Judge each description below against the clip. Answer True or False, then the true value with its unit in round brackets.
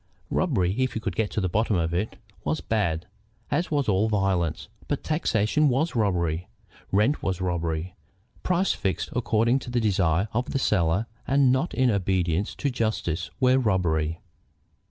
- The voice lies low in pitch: True (105 Hz)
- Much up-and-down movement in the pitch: True (6.2 semitones)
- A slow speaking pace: False (160 wpm)